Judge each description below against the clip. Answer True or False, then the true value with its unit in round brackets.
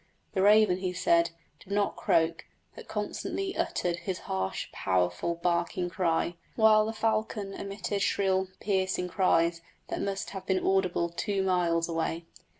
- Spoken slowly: False (145 wpm)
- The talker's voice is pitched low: False (185 Hz)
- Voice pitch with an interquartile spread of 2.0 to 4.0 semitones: True (2.8 semitones)